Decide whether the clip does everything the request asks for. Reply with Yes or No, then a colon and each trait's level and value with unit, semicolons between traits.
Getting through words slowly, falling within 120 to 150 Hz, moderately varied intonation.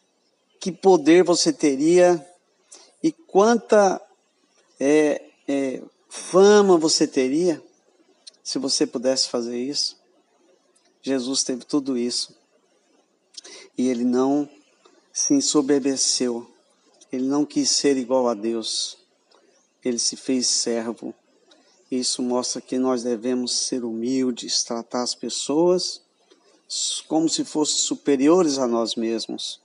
Yes: slow, 105 wpm; low, 135 Hz; average, 4.7 semitones